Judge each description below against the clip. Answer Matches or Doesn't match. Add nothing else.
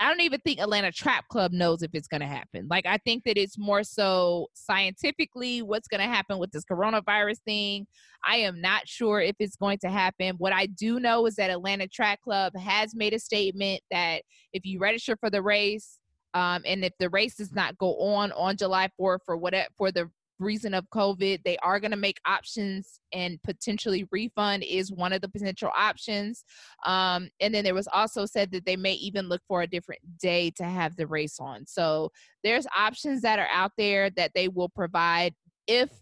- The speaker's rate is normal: Doesn't match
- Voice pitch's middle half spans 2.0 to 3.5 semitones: Matches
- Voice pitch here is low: Doesn't match